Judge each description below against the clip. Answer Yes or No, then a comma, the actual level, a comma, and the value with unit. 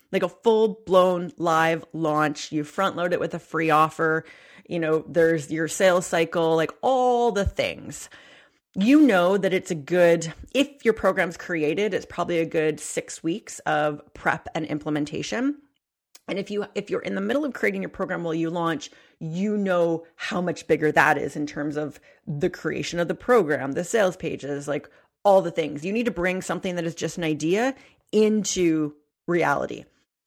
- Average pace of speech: Yes, average, 185 wpm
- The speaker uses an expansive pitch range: No, average, 3.5 semitones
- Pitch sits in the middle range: Yes, medium, 170 Hz